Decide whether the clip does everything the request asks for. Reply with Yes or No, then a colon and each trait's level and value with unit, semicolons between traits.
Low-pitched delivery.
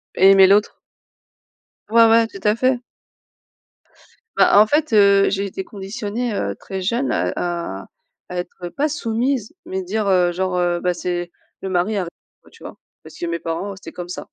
No: high, 195 Hz